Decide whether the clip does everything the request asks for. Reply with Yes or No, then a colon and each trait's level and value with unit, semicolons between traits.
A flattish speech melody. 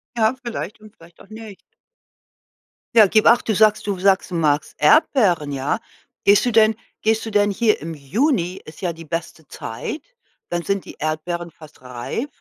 No: average, 5.0 semitones